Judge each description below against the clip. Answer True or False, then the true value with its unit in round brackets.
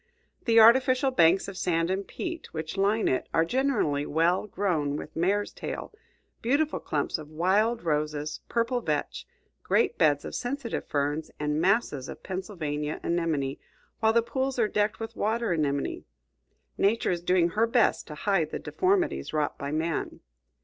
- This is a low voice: False (185 Hz)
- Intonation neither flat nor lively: False (6.9 semitones)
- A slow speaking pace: False (155 wpm)